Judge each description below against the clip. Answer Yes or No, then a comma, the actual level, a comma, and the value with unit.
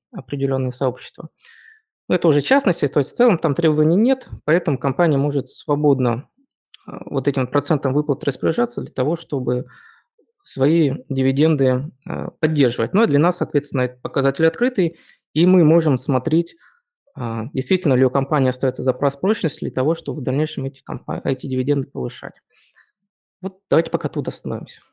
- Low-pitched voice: No, medium, 145 Hz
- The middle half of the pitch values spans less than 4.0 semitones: No, average, 4.4 semitones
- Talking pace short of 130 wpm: No, average, 145 wpm